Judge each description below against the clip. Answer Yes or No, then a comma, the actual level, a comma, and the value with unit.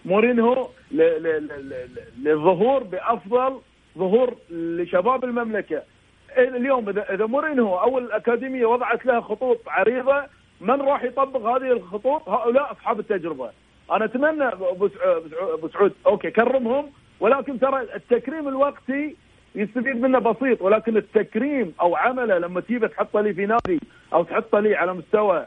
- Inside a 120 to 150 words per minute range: Yes, average, 130 wpm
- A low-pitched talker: No, high, 235 Hz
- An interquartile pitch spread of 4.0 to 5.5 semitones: Yes, average, 4.4 semitones